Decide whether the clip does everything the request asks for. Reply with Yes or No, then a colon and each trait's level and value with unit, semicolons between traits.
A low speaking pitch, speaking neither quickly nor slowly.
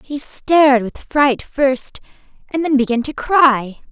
No: very high, 270 Hz; average, 155 wpm